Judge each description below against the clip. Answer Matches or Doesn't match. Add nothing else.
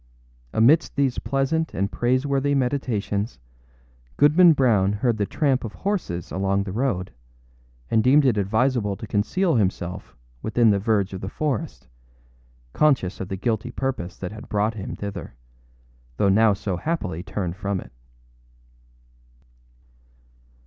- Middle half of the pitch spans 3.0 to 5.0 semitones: Doesn't match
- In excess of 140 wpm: Doesn't match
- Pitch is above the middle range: Doesn't match